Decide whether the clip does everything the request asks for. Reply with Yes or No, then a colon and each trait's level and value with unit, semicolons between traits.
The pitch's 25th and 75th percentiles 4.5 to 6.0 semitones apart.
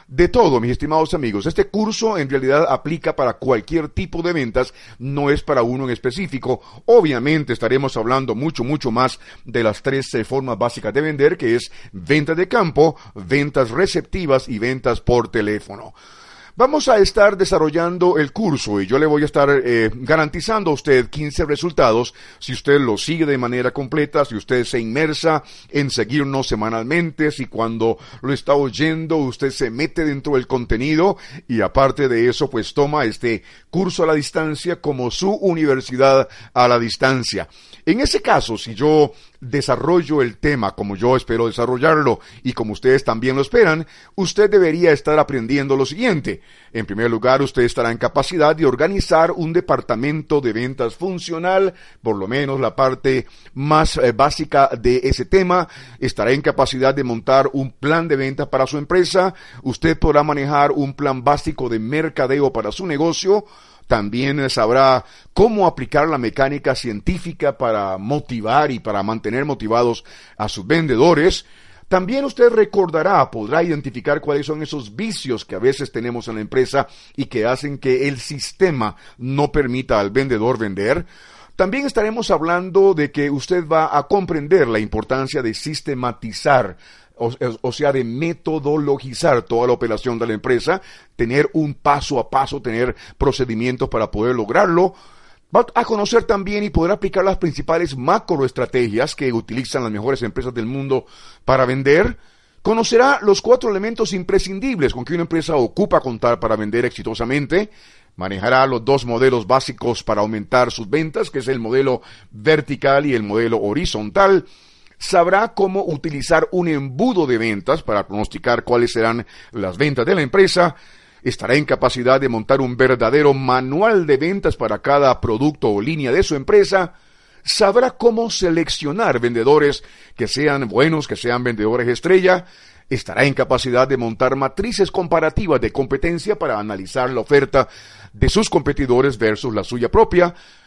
Yes: average, 4.9 semitones